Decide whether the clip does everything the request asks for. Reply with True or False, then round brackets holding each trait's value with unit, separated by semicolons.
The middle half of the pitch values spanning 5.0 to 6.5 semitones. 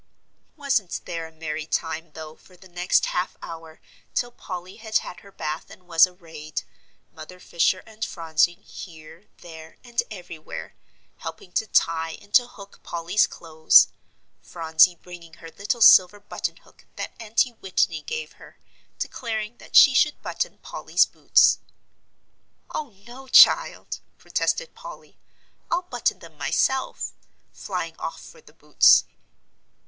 True (5.5 semitones)